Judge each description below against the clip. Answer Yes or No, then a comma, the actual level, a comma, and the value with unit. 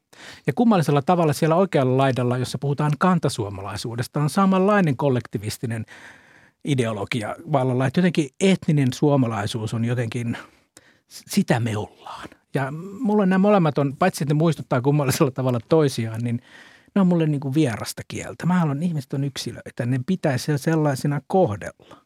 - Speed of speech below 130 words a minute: No, average, 140 wpm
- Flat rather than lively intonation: No, average, 4.9 semitones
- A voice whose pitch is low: No, medium, 145 Hz